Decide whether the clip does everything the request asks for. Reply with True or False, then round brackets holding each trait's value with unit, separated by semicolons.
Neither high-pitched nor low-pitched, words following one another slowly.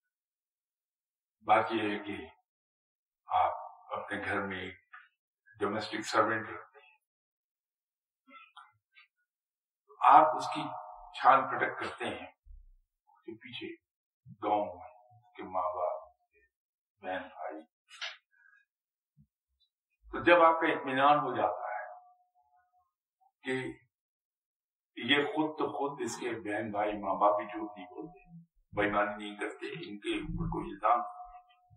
True (155 Hz; 105 wpm)